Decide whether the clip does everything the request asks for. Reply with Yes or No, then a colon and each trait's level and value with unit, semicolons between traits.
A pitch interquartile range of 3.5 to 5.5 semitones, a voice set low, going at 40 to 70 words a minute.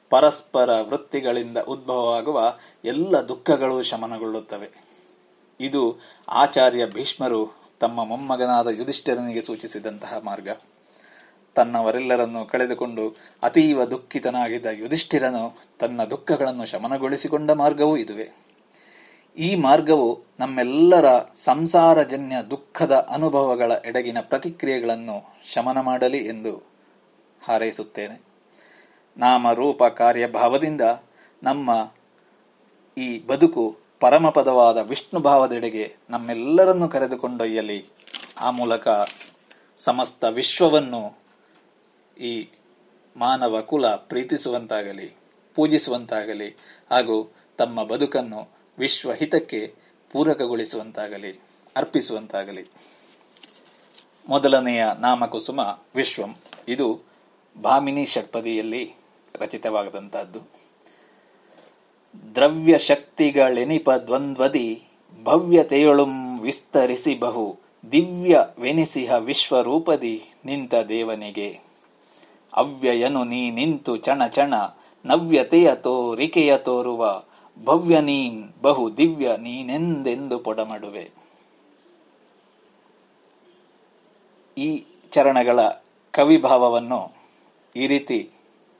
Yes: average, 4.2 semitones; low, 125 Hz; slow, 65 wpm